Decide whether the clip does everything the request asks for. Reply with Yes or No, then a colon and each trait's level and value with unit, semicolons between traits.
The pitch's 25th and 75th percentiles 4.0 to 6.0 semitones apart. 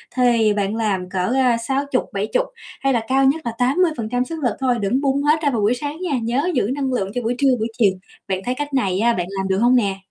Yes: average, 4.4 semitones